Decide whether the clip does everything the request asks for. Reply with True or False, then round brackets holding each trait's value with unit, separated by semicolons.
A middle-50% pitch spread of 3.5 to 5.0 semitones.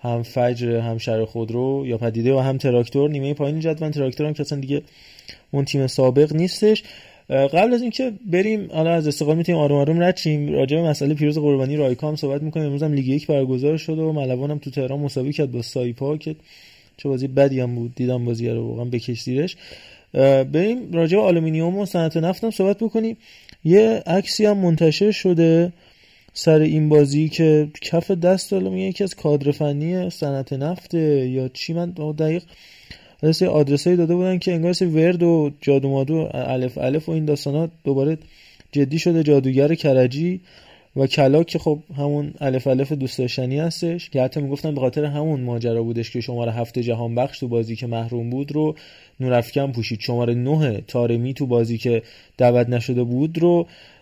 True (4.2 semitones)